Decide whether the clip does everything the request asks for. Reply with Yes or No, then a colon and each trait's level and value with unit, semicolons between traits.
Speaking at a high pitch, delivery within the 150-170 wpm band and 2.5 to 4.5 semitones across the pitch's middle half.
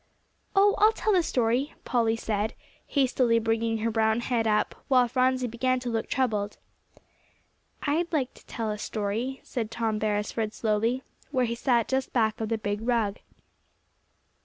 Yes: high, 230 Hz; average, 160 wpm; average, 2.8 semitones